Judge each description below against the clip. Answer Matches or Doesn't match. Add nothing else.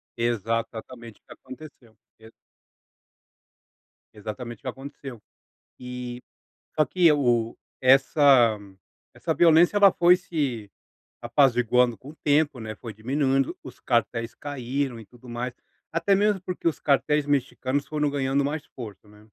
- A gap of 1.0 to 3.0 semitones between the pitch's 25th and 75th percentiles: Doesn't match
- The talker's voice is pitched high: Doesn't match